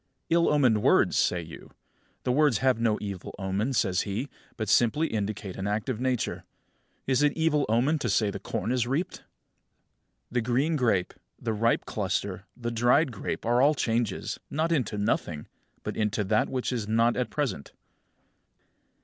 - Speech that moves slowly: No, average, 175 wpm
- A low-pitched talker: Yes, low, 115 Hz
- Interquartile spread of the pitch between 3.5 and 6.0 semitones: Yes, average, 4.2 semitones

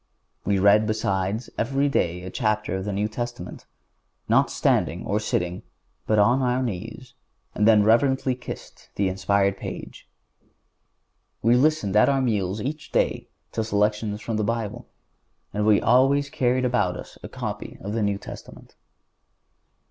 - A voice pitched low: Yes, low, 110 Hz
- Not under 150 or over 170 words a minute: Yes, average, 155 wpm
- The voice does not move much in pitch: No, average, 3.5 semitones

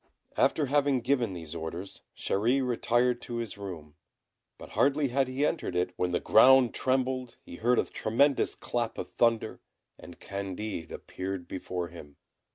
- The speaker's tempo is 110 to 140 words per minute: No, average, 155 wpm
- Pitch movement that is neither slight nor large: No, wide, 6.1 semitones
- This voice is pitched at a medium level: No, low, 115 Hz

